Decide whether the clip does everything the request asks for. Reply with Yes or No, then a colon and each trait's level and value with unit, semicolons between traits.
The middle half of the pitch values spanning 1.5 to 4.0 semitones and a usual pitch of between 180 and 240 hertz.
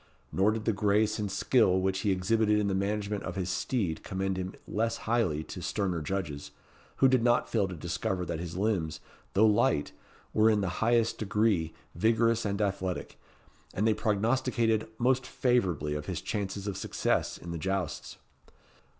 No: average, 3.3 semitones; low, 100 Hz